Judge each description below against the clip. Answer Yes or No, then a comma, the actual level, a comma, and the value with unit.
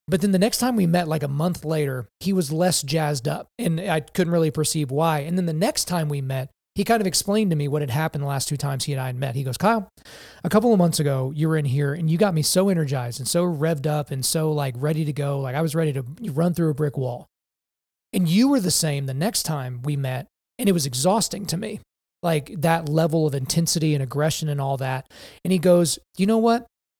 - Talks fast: Yes, fast, 260 wpm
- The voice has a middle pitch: Yes, medium, 160 Hz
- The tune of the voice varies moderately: Yes, average, 4.0 semitones